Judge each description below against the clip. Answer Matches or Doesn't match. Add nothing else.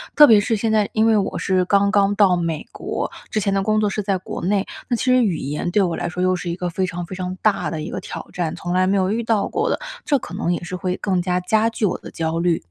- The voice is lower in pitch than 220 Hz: Matches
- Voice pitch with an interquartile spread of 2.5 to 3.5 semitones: Matches